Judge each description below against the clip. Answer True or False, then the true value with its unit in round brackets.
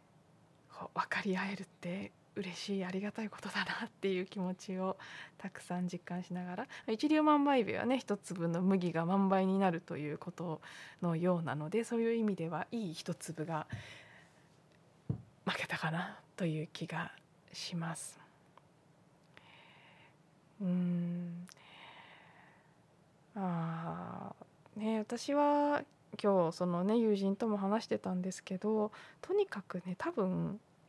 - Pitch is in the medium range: True (180 Hz)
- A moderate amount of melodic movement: True (3.6 semitones)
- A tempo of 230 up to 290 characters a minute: True (240 characters per minute)